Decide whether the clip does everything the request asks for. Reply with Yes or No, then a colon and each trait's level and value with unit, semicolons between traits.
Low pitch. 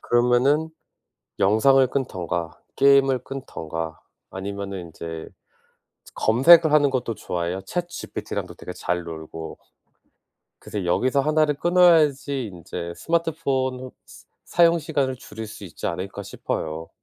Yes: low, 125 Hz